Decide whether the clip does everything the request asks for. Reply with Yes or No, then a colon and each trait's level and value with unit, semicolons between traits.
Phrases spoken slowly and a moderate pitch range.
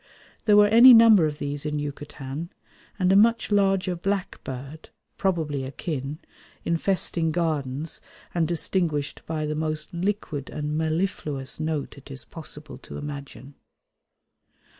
Yes: slow, 130 wpm; average, 4.1 semitones